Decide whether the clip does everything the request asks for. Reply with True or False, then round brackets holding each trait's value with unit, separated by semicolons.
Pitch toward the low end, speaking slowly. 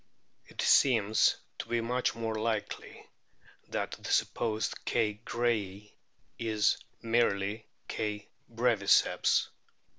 True (110 Hz; 95 wpm)